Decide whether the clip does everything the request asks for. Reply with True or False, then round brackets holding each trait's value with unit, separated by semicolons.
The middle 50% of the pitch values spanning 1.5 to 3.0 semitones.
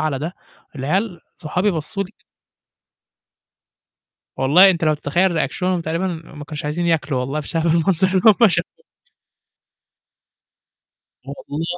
False (3.5 semitones)